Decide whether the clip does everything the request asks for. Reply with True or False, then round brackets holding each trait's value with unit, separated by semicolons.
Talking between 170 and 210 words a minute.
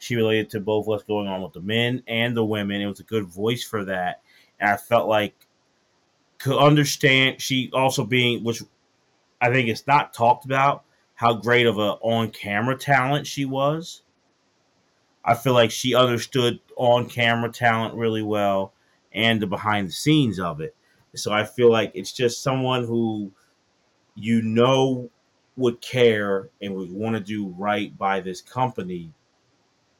False (160 wpm)